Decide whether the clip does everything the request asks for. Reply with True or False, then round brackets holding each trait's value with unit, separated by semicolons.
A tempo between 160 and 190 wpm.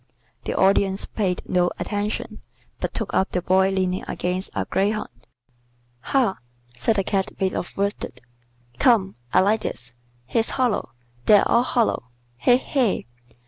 False (140 wpm)